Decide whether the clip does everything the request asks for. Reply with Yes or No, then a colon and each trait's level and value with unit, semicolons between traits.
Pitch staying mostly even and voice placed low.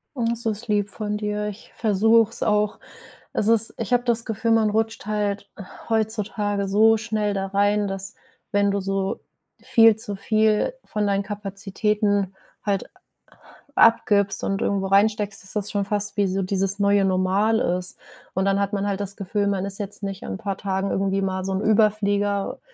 No: narrow, 1.5 semitones; high, 205 Hz